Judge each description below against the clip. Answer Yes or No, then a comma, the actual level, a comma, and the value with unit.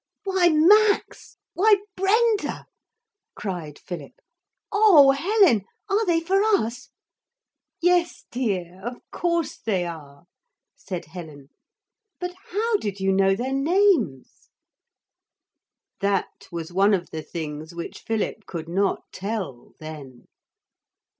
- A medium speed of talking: No, slow, 110 wpm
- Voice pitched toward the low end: No, high, 220 Hz